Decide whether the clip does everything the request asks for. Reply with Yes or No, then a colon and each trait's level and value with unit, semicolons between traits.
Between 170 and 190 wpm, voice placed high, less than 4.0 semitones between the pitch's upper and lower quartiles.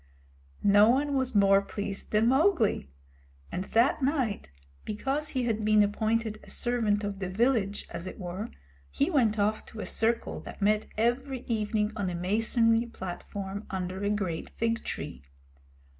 No: average, 160 wpm; high, 215 Hz; average, 2.9 semitones